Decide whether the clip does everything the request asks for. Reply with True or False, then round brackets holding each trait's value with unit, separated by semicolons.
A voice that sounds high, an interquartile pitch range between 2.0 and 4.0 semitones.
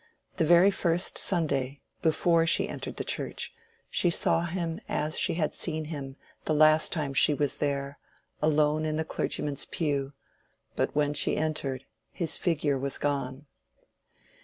False (155 Hz; 2.6 semitones)